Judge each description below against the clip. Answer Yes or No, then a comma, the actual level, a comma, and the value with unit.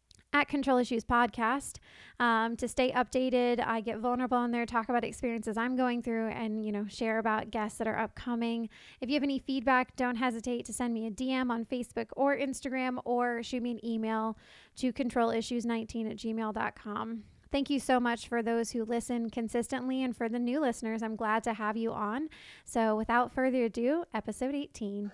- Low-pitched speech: No, high, 235 Hz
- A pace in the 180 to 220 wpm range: Yes, average, 190 wpm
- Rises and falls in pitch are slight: Yes, narrow, 2.0 semitones